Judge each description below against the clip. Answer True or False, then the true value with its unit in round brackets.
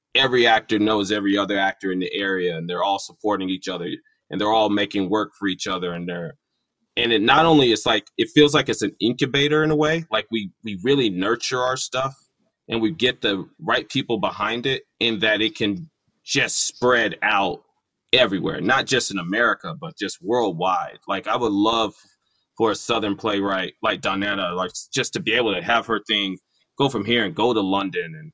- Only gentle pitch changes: False (5.3 semitones)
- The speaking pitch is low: True (110 Hz)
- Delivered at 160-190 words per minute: False (205 wpm)